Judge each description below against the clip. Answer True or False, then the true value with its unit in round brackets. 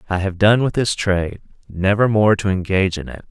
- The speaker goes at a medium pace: False (220 wpm)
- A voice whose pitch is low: True (100 Hz)